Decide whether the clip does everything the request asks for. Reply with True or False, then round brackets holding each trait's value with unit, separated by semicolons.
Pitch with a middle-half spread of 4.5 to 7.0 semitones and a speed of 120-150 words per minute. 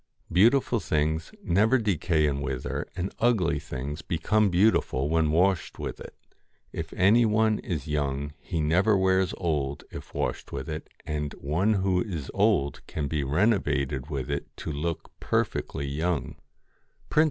True (5.0 semitones; 145 wpm)